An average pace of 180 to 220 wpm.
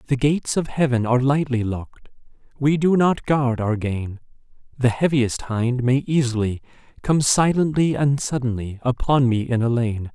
No: average, 160 wpm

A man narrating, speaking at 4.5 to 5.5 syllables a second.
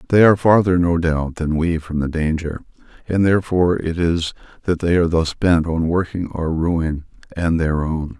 Yes: male; 4.9 syllables/s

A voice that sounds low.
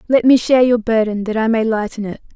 No: high, 225 Hz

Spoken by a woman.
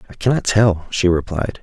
No: male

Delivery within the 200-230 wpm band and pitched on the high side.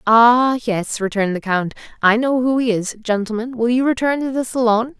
Yes: fast, 205 wpm; high, 235 Hz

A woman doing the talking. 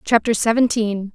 Yes: female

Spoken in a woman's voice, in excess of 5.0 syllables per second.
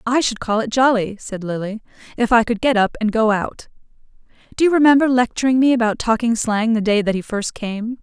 Yes: female; 5.5 syllables/s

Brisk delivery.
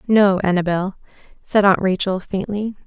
No: slow, 125 wpm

